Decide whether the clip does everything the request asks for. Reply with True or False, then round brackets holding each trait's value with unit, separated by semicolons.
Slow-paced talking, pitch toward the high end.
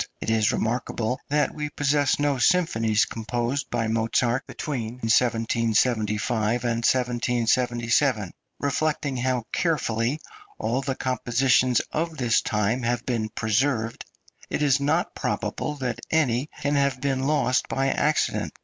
False (125 wpm; 125 Hz)